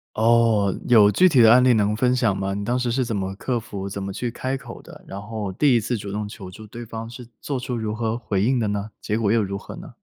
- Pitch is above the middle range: No, low, 110 Hz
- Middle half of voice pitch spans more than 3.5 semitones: No, average, 3.0 semitones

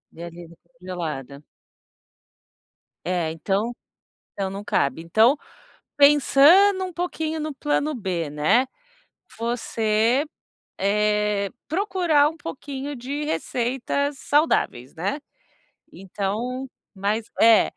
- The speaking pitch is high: Yes, high, 230 Hz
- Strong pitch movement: Yes, wide, 7.2 semitones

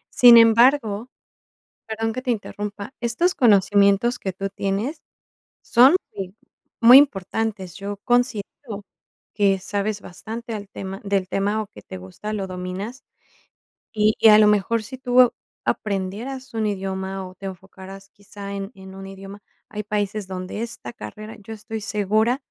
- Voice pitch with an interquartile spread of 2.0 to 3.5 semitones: Yes, average, 2.7 semitones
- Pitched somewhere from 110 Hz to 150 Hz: No, high, 205 Hz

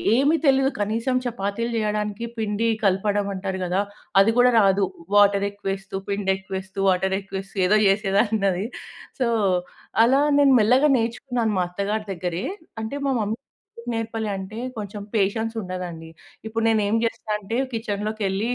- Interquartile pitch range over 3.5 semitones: No, average, 2.7 semitones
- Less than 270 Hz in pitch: Yes, high, 210 Hz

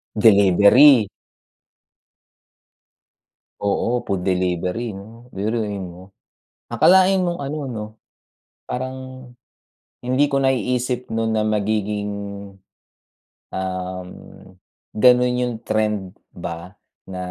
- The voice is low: Yes, low, 110 Hz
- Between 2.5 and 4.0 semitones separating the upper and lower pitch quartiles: No, average, 4.6 semitones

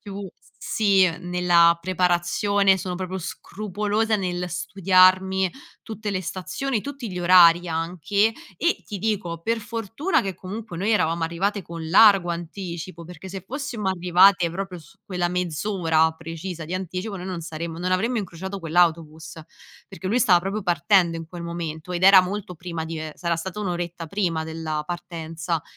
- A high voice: No, medium, 180 Hz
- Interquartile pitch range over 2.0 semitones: Yes, average, 2.7 semitones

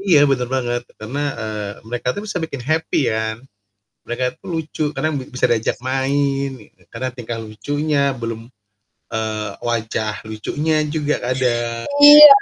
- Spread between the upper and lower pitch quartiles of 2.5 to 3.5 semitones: No, average, 4.6 semitones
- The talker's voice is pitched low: Yes, low, 125 Hz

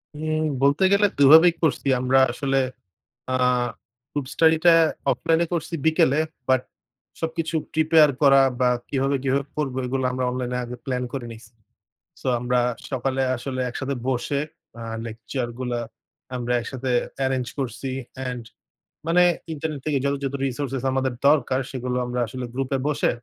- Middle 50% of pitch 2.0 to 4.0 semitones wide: Yes, average, 2.9 semitones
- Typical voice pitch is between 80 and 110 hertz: No, low, 135 Hz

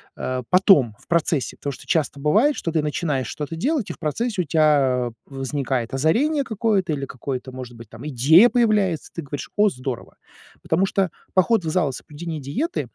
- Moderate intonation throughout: No, wide, 6.2 semitones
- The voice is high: No, medium, 155 Hz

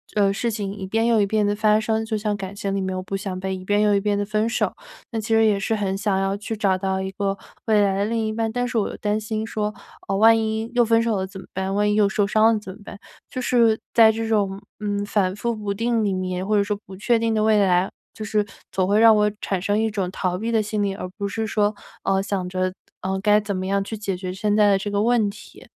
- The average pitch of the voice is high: Yes, high, 205 Hz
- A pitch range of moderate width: No, narrow, 2.0 semitones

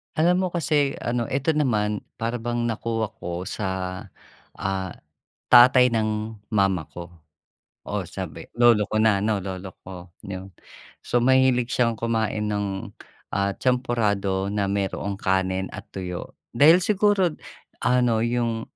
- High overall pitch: No, low, 110 Hz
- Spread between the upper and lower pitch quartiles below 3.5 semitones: No, average, 4.0 semitones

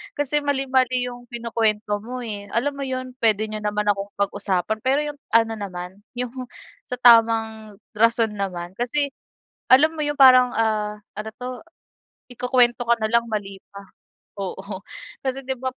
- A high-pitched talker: Yes, high, 230 Hz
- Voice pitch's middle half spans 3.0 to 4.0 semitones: Yes, average, 3.4 semitones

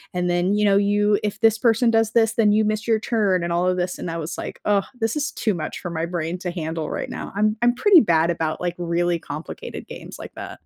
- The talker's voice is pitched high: Yes, high, 195 Hz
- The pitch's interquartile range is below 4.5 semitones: Yes, average, 4.1 semitones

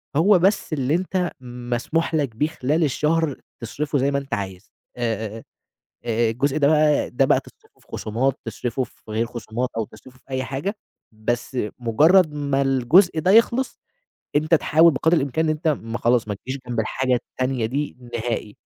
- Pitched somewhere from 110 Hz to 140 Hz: Yes, low, 135 Hz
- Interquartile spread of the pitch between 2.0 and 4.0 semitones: No, average, 4.6 semitones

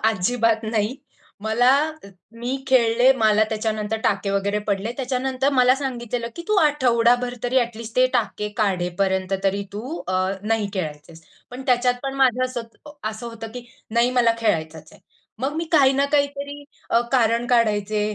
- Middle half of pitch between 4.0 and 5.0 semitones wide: No, average, 3.3 semitones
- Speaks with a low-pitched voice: No, high, 235 Hz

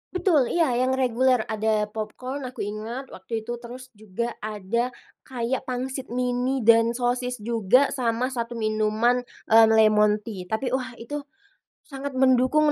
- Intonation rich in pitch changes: No, average, 2.8 semitones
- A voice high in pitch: Yes, high, 240 Hz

